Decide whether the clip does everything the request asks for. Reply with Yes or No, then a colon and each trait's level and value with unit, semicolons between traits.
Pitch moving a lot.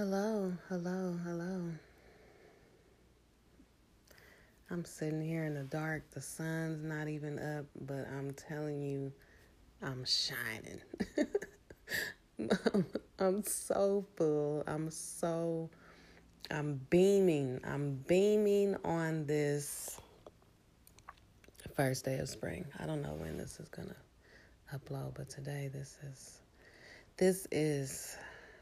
No: average, 4.1 semitones